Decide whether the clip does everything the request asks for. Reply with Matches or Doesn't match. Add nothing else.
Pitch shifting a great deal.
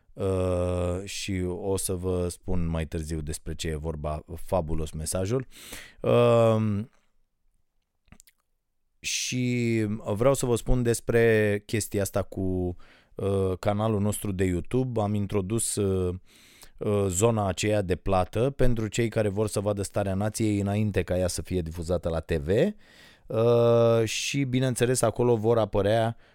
Doesn't match